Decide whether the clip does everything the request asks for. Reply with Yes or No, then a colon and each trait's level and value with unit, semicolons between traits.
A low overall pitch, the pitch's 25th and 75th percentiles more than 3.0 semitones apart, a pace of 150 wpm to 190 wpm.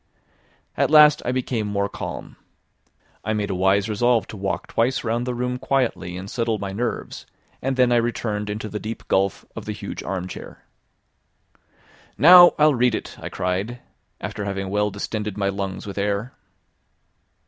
Yes: low, 105 Hz; average, 3.6 semitones; average, 165 wpm